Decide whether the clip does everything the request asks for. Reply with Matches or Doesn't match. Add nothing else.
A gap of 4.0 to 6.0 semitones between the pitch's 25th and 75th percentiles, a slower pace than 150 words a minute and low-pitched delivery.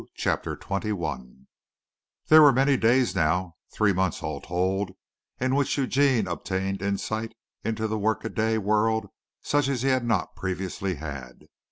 Matches